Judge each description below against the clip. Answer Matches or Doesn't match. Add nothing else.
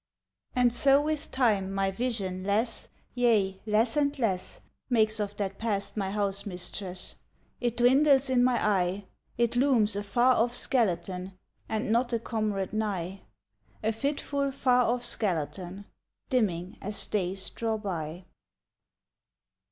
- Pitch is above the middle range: Matches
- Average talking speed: Doesn't match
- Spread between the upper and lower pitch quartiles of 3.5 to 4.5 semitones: Matches